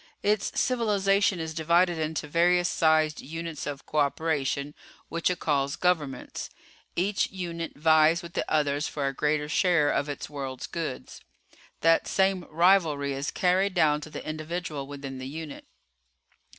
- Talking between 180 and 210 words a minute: No, average, 145 wpm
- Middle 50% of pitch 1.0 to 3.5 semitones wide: Yes, average, 3.2 semitones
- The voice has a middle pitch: Yes, medium, 160 Hz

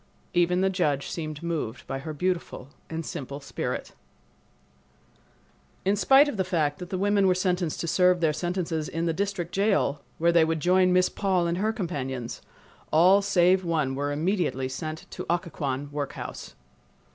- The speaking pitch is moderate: Yes, medium, 170 Hz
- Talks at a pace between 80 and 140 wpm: No, average, 165 wpm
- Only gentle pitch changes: No, average, 3.6 semitones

